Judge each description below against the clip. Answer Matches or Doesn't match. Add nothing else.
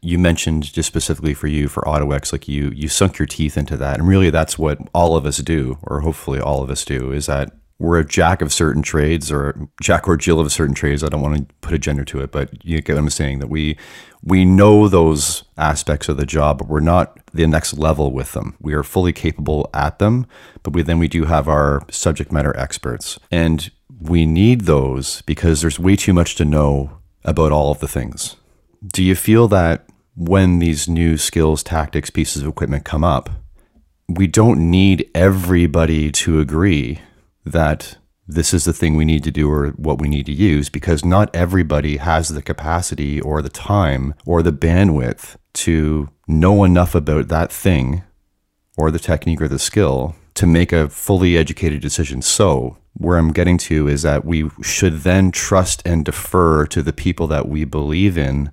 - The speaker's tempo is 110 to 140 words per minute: Doesn't match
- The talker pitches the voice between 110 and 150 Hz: Doesn't match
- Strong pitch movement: Doesn't match